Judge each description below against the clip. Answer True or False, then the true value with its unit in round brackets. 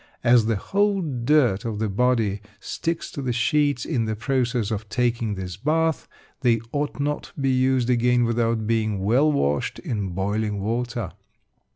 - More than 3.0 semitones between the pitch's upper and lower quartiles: True (3.6 semitones)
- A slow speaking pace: False (165 wpm)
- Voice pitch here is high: False (120 Hz)